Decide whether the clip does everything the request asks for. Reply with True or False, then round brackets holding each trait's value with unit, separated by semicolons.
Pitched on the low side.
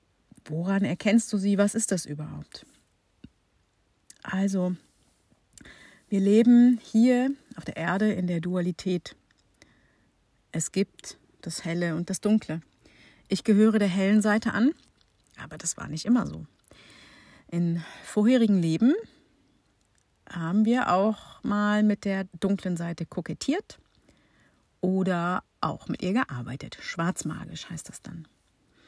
False (190 Hz)